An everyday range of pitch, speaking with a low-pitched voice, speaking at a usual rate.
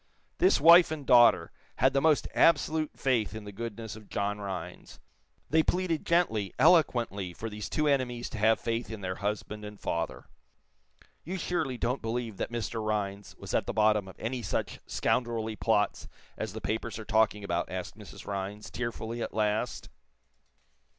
Yes: average, 3.6 semitones; low, 110 Hz; average, 170 wpm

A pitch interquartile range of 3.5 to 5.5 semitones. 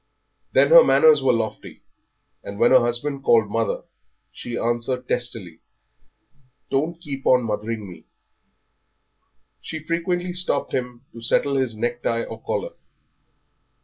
Yes: average, 3.9 semitones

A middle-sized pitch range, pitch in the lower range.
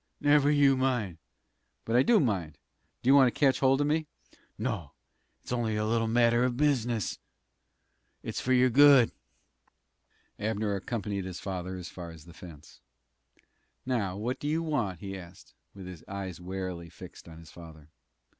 No: wide, 6.0 semitones; low, 110 Hz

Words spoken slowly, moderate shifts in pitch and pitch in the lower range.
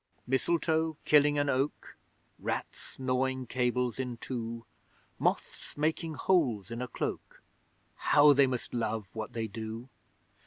Yes: slow, 125 wpm; average, 3.8 semitones; low, 130 Hz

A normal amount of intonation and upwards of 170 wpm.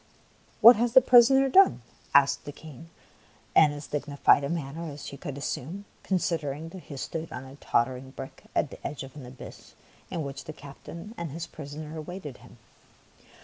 Yes: average, 3.4 semitones; average, 190 wpm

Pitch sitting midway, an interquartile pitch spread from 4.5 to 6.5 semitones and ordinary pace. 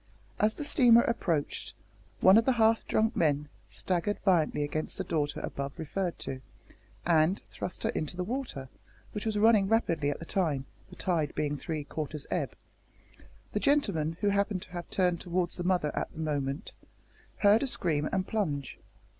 Yes: medium, 175 Hz; wide, 5.4 semitones; average, 170 wpm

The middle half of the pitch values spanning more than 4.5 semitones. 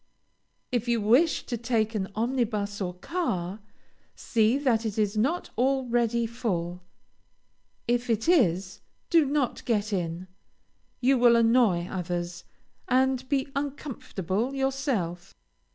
Yes: average, 5.2 semitones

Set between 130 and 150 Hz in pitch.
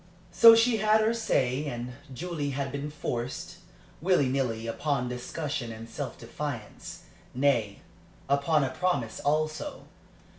Yes: medium, 140 Hz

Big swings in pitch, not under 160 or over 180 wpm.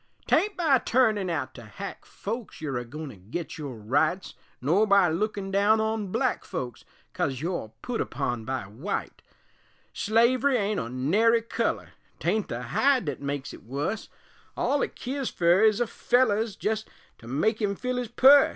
Yes: wide, 8.3 semitones; average, 170 wpm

